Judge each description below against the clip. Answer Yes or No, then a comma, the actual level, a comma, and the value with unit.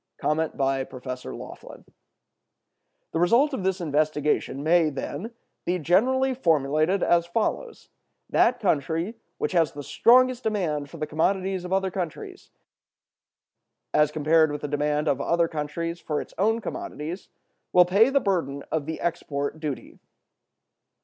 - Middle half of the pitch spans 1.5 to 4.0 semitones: No, average, 4.5 semitones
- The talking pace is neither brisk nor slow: No, slow, 130 wpm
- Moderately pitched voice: Yes, medium, 165 Hz